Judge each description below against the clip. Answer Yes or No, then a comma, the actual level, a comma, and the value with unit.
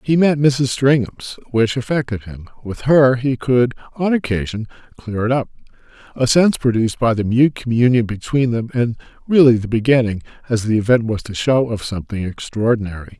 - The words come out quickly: No, average, 170 wpm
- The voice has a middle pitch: No, low, 120 Hz